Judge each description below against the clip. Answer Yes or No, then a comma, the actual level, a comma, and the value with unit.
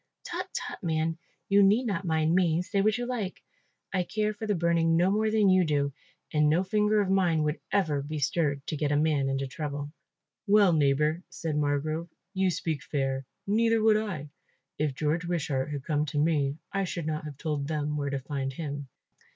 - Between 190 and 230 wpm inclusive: Yes, average, 200 wpm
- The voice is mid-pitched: Yes, medium, 160 Hz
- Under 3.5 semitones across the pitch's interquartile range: No, average, 4.7 semitones